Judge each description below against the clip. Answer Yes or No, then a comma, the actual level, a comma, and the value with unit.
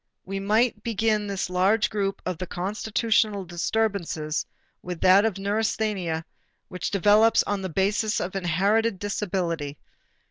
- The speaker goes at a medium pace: No, slow, 120 wpm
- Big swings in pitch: No, average, 2.9 semitones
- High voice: Yes, high, 195 Hz